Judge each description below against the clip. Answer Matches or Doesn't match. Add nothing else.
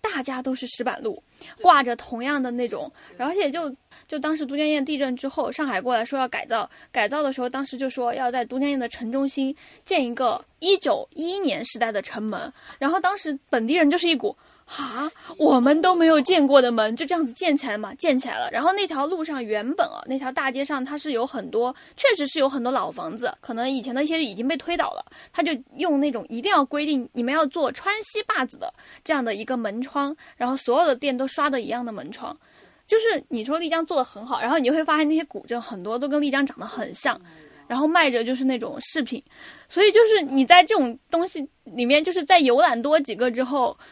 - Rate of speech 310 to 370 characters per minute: Matches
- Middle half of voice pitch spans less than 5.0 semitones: Matches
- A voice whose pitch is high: Matches